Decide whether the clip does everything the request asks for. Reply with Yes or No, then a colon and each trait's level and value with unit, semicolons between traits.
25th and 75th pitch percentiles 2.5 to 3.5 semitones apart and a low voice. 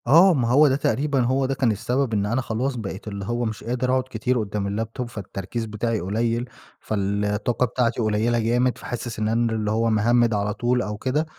Yes: average, 2.9 semitones; low, 115 Hz